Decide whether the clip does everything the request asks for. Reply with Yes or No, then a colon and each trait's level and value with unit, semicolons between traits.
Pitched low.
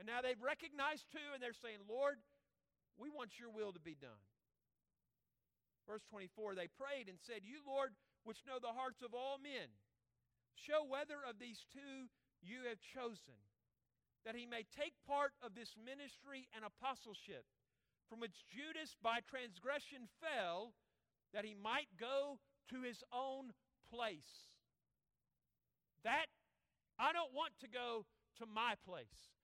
No: high, 240 Hz